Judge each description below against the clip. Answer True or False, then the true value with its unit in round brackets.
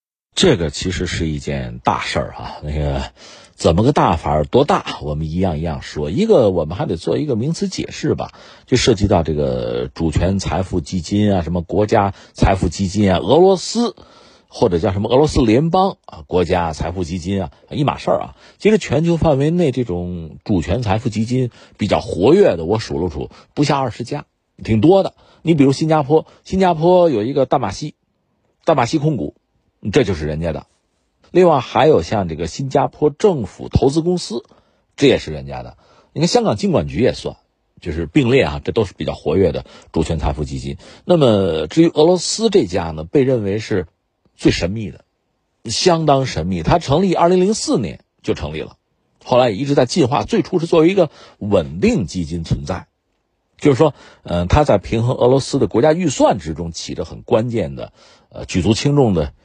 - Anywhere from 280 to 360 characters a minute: True (285 characters per minute)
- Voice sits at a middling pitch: False (105 Hz)